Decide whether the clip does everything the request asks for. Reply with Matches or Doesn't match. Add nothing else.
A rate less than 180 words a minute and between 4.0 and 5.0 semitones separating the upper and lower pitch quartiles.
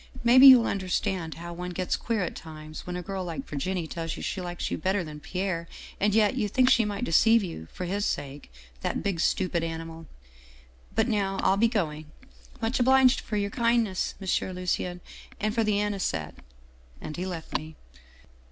Doesn't match